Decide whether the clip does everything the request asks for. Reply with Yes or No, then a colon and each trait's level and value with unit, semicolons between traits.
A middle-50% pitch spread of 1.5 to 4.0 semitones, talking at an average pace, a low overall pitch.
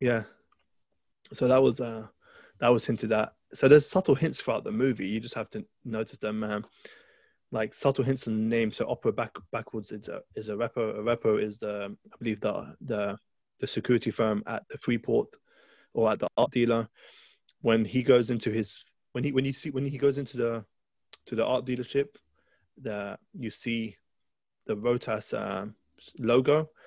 Yes: average, 3.1 semitones; average, 185 wpm; low, 115 Hz